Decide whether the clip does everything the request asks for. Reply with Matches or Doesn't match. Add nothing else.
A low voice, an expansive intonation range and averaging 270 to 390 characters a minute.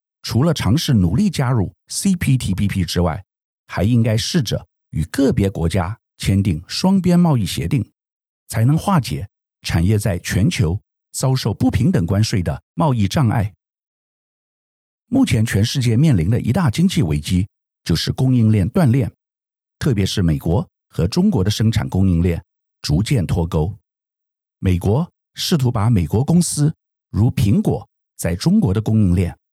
Doesn't match